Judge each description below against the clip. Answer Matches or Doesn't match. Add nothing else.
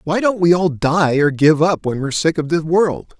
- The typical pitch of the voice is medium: Matches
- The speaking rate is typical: Doesn't match